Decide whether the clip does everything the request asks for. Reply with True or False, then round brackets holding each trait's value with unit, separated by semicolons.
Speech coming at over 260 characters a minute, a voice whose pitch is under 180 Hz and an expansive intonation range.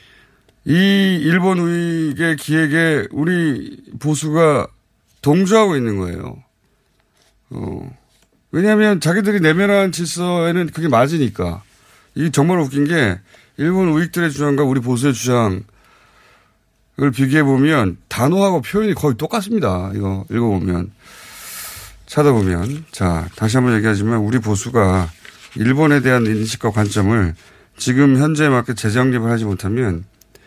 True (275 characters per minute; 135 Hz; 7.0 semitones)